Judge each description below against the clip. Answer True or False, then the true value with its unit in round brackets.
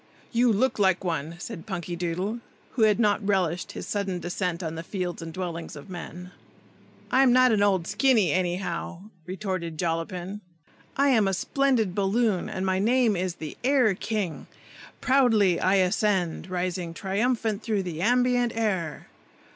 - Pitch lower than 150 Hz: False (190 Hz)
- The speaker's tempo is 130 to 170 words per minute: True (150 wpm)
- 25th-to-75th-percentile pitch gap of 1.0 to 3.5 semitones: False (4.0 semitones)